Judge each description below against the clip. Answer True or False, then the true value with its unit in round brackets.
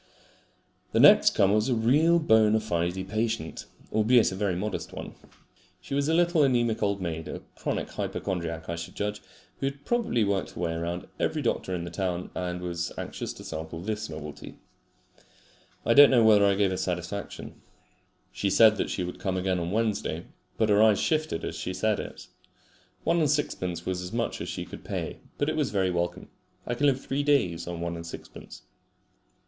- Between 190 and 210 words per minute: True (195 wpm)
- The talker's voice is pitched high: False (100 Hz)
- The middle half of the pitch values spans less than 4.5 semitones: False (5.0 semitones)